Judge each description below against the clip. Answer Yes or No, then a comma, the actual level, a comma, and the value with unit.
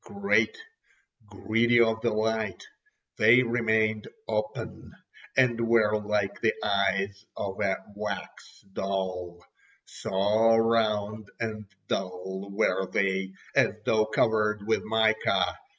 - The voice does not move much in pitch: Yes, narrow, 2.2 semitones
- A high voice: No, low, 105 Hz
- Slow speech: Yes, slow, 105 wpm